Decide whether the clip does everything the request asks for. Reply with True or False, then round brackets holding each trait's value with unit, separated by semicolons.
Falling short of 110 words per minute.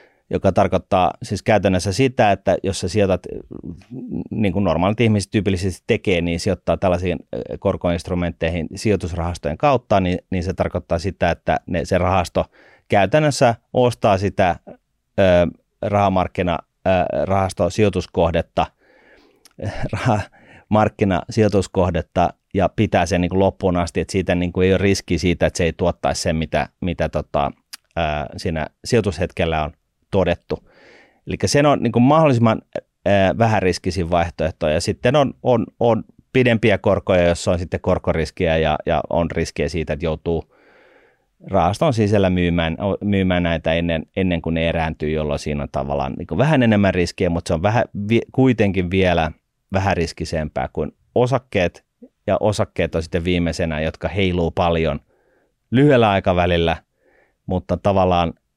False (130 wpm)